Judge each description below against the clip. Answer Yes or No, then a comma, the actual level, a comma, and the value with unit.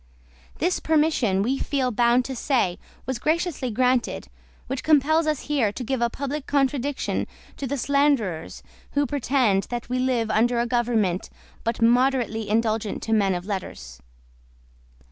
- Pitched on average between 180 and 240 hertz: No, very high, 250 Hz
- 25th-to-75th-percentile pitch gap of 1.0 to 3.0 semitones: No, average, 3.9 semitones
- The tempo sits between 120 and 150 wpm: Yes, average, 145 wpm